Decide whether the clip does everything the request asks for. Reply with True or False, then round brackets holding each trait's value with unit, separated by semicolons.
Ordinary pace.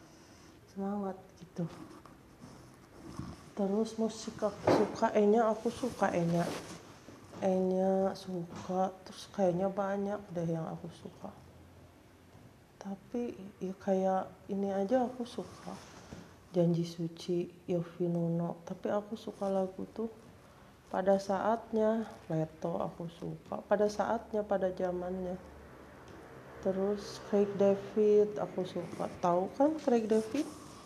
True (100 wpm)